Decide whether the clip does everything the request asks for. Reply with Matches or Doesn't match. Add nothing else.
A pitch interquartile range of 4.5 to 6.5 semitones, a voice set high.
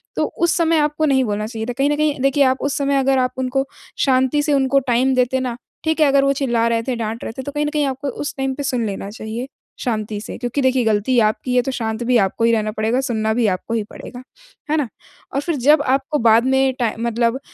Doesn't match